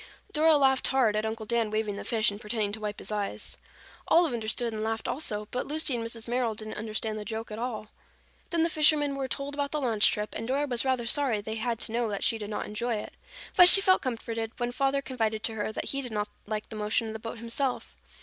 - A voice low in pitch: No, high, 230 Hz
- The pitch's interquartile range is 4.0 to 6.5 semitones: No, average, 3.5 semitones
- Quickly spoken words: Yes, fast, 245 wpm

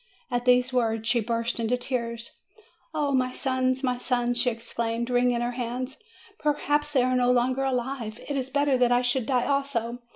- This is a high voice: Yes, very high, 250 Hz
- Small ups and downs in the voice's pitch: Yes, narrow, 1.8 semitones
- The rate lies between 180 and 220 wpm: Yes, average, 185 wpm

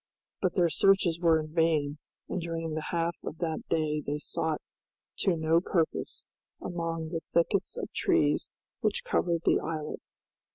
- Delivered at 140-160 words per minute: Yes, average, 150 wpm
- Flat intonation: Yes, narrow, 1.5 semitones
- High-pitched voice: No, medium, 165 Hz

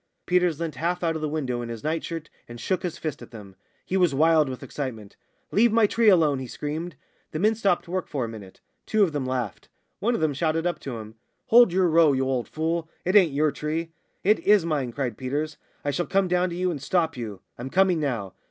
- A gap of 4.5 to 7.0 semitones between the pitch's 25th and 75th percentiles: Yes, average, 5.2 semitones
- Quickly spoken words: Yes, fast, 235 wpm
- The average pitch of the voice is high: No, medium, 155 Hz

